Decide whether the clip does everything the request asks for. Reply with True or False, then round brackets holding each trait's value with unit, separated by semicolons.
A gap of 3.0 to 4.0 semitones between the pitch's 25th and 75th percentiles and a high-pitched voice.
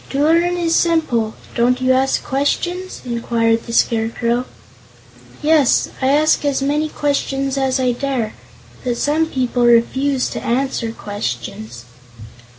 True (3.7 semitones; 260 Hz)